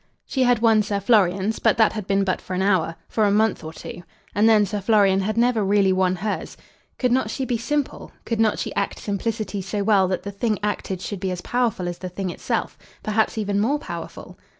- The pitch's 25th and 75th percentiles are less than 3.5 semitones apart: Yes, average, 2.7 semitones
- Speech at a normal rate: No, fast, 225 wpm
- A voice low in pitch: No, high, 205 Hz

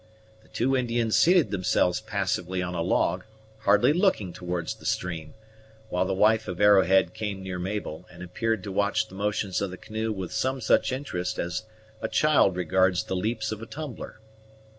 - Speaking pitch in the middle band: No, low, 100 Hz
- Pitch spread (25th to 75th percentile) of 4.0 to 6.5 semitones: No, average, 3.6 semitones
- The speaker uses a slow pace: No, average, 180 wpm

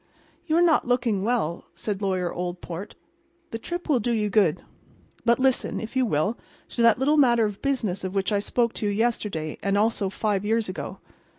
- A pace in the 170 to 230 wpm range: Yes, average, 195 wpm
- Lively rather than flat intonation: No, average, 3.8 semitones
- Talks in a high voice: Yes, high, 215 Hz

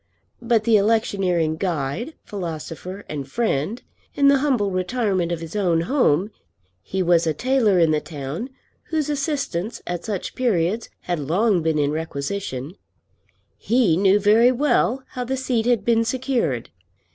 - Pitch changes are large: Yes, wide, 6.5 semitones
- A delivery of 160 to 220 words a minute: No, average, 145 wpm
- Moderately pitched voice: No, high, 200 Hz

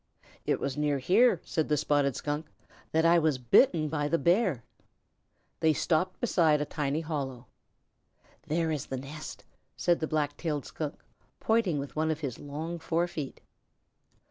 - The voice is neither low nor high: Yes, medium, 155 Hz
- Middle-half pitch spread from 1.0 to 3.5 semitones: Yes, narrow, 2.5 semitones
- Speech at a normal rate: Yes, average, 155 wpm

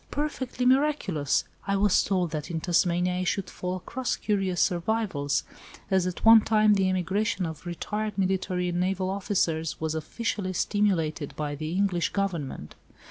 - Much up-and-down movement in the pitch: No, average, 3.3 semitones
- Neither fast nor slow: Yes, average, 150 wpm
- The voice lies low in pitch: No, medium, 185 Hz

